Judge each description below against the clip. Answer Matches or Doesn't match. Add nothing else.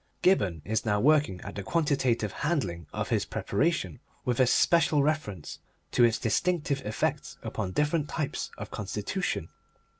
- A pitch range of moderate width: Doesn't match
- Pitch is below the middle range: Matches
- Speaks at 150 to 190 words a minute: Doesn't match